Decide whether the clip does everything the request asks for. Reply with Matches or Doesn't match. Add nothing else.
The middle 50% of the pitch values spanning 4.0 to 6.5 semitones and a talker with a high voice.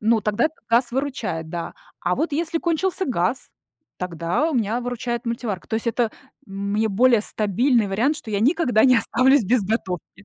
Matches